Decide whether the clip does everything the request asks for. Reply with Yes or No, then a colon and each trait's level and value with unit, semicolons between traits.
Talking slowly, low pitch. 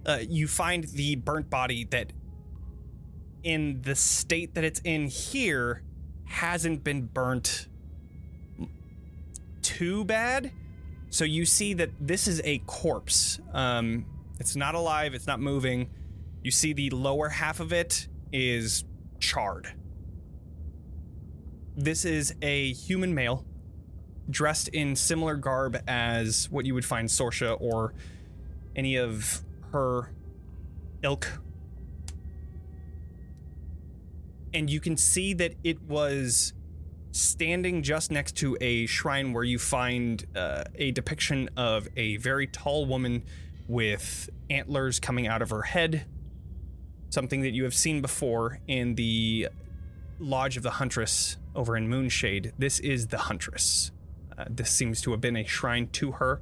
Yes: slow, 130 wpm; low, 115 Hz